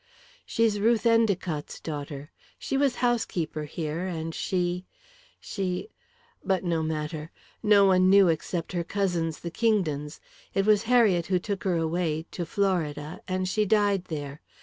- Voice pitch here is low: No, medium, 180 Hz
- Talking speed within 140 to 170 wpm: Yes, average, 145 wpm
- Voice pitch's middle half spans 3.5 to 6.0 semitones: Yes, average, 4.0 semitones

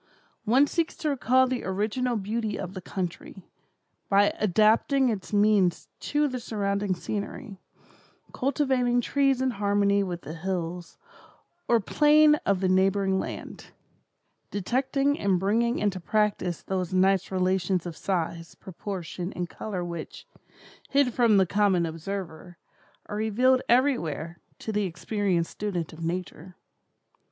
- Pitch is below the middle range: No, high, 200 Hz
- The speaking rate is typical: No, slow, 130 wpm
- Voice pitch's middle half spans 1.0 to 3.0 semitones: No, average, 4.6 semitones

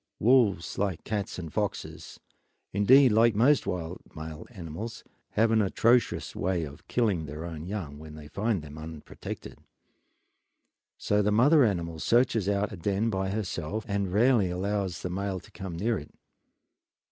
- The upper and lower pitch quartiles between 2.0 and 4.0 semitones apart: No, average, 4.8 semitones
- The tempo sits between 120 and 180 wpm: Yes, average, 160 wpm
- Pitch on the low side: Yes, low, 100 Hz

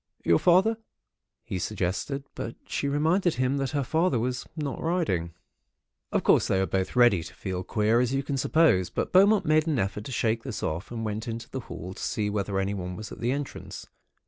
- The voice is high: No, low, 120 Hz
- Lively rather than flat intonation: Yes, wide, 6.8 semitones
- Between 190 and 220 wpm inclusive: Yes, fast, 205 wpm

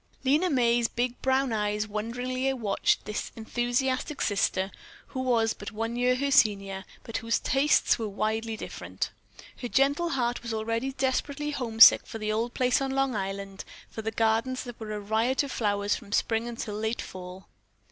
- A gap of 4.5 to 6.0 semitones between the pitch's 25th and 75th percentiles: No, average, 3.3 semitones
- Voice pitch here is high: Yes, high, 230 Hz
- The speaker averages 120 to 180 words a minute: Yes, average, 170 wpm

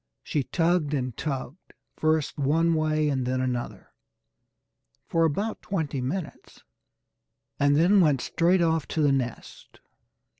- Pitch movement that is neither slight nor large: Yes, average, 3.4 semitones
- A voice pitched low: No, medium, 155 Hz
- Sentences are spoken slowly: Yes, slow, 125 wpm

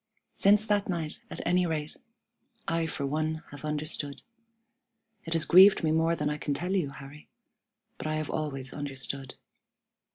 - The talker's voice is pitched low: No, medium, 155 Hz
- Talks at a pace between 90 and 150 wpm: No, average, 160 wpm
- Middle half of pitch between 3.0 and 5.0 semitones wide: No, narrow, 2.6 semitones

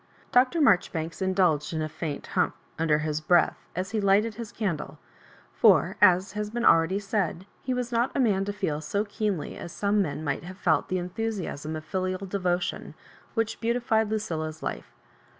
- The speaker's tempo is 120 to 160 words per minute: No, average, 185 wpm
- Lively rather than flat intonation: No, average, 4.7 semitones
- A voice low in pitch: No, high, 190 Hz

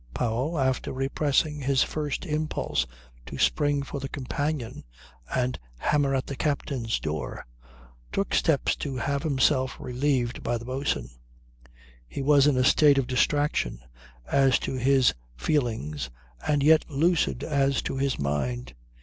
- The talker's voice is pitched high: No, low, 135 Hz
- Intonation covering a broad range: No, average, 2.8 semitones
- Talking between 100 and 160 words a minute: Yes, average, 140 wpm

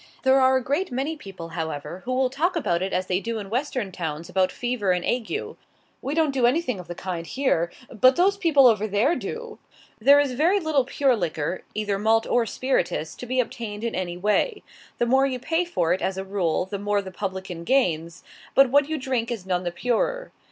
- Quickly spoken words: Yes, fast, 220 wpm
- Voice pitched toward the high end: Yes, high, 235 Hz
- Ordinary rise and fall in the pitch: No, wide, 6.4 semitones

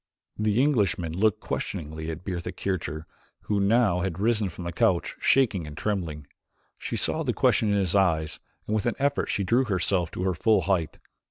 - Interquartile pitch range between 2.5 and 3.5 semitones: No, average, 4.1 semitones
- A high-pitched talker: No, very low, 95 Hz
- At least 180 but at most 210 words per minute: Yes, average, 185 wpm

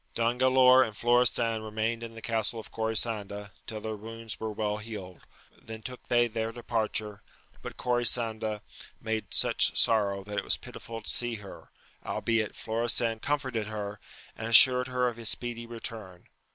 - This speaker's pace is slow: No, average, 165 wpm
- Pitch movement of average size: No, narrow, 1.7 semitones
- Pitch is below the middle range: Yes, low, 115 Hz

